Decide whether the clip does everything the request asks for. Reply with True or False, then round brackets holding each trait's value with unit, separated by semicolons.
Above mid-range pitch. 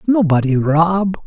False (170 Hz)